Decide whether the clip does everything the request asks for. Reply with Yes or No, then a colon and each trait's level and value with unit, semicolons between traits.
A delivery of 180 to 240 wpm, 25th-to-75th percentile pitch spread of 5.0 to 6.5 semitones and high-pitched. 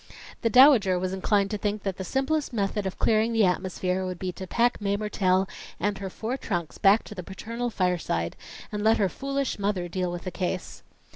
No: fast, 205 wpm; average, 3.2 semitones; high, 200 Hz